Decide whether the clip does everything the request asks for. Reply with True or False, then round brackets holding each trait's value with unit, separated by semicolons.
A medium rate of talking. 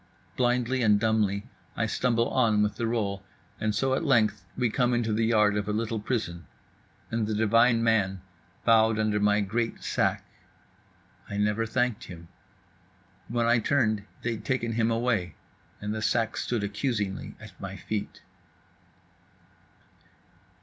True (145 wpm)